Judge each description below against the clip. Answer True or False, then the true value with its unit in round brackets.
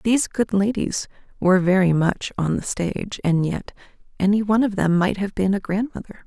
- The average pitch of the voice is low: False (195 Hz)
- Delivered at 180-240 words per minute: True (200 wpm)